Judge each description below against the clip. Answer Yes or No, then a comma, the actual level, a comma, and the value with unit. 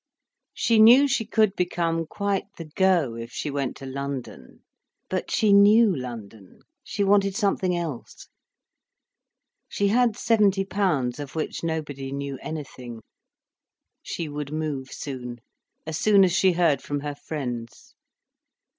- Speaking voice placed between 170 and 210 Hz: No, medium, 160 Hz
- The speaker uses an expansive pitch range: Yes, wide, 6.5 semitones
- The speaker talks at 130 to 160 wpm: Yes, slow, 135 wpm